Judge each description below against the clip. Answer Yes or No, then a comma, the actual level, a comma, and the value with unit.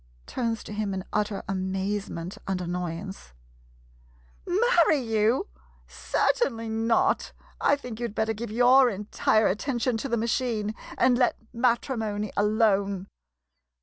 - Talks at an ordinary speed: No, slow, 125 wpm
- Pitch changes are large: No, average, 3.3 semitones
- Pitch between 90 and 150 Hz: No, high, 220 Hz